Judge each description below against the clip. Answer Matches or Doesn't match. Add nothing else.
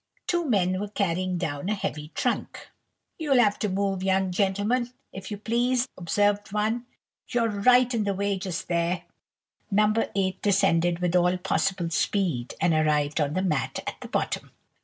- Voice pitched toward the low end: Doesn't match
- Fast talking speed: Doesn't match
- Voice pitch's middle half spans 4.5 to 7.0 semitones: Doesn't match